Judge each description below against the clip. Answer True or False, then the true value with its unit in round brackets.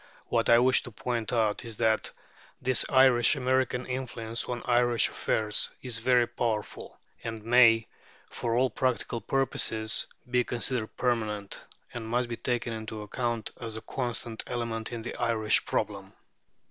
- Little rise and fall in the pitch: True (1.8 semitones)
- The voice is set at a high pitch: False (120 Hz)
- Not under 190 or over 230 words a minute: False (145 wpm)